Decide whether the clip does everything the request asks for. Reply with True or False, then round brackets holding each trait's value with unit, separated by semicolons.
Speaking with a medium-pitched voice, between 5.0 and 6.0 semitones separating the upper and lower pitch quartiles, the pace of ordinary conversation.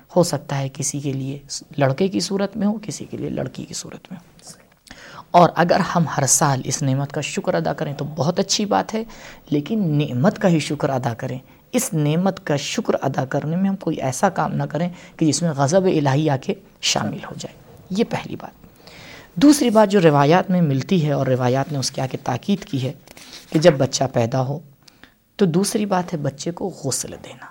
False (155 Hz; 5.3 semitones; 215 wpm)